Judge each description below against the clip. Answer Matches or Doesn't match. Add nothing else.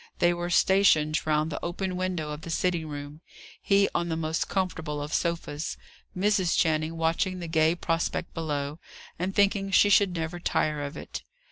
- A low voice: Doesn't match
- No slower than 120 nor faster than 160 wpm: Doesn't match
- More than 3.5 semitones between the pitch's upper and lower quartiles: Doesn't match